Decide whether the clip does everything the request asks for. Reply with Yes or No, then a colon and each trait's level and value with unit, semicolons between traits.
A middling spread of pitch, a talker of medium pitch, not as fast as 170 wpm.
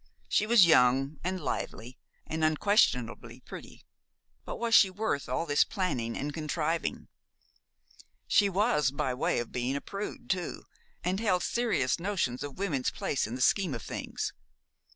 No: wide, 6.8 semitones; medium, 160 Hz; average, 150 wpm